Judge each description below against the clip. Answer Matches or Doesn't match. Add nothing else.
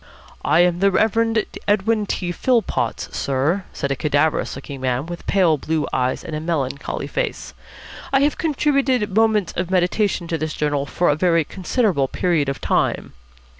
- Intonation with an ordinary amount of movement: Doesn't match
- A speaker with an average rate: Matches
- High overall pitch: Doesn't match